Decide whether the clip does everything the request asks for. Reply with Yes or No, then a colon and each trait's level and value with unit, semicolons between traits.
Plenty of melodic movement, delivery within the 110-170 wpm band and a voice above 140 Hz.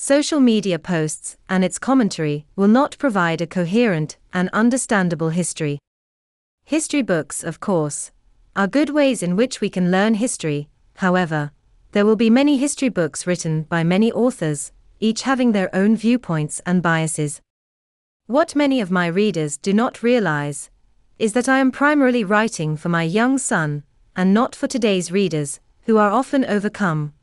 Yes: wide, 7.4 semitones; average, 160 wpm; medium, 185 Hz